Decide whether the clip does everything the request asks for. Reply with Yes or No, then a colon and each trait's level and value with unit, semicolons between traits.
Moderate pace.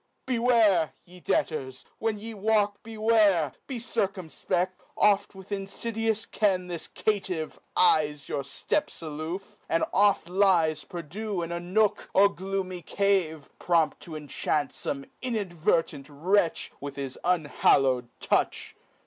No: slow, 125 wpm